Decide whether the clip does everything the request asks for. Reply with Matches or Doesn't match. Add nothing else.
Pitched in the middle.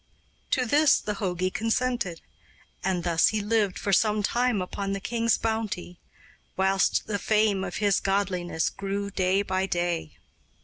Doesn't match